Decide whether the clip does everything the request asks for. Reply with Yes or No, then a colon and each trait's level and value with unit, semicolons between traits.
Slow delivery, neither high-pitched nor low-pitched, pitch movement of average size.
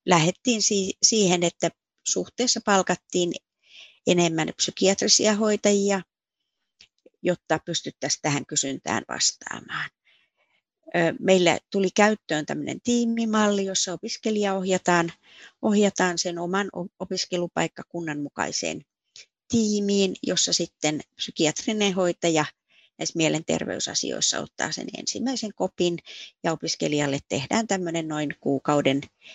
Yes: slow, 90 wpm; medium, 180 Hz; average, 3.8 semitones